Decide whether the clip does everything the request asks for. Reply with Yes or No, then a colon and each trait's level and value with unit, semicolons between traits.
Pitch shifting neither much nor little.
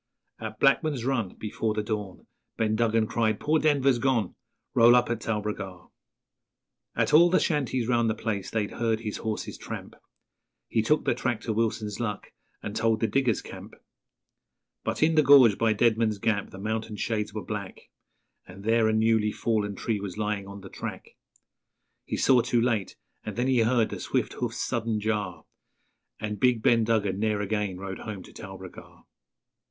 No: narrow, 2.2 semitones